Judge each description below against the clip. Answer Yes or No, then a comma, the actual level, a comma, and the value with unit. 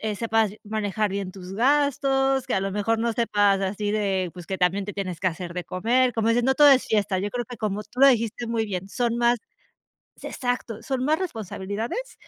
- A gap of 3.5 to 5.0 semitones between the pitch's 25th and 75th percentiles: Yes, average, 3.9 semitones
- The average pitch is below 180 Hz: No, high, 220 Hz